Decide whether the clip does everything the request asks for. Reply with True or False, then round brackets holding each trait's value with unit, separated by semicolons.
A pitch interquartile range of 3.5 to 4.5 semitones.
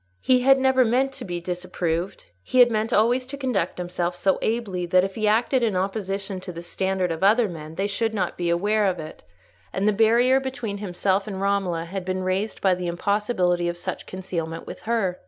True (3.8 semitones)